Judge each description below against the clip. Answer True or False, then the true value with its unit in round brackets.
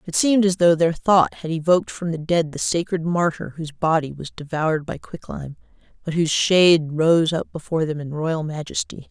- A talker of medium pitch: True (165 Hz)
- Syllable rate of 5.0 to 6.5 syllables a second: True (5.5 syllables/s)